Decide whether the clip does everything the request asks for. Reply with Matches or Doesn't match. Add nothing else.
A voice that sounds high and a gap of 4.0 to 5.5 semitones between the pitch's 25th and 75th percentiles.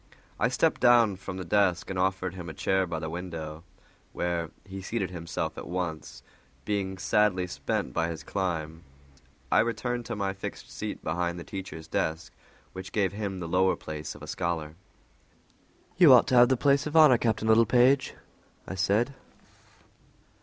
Doesn't match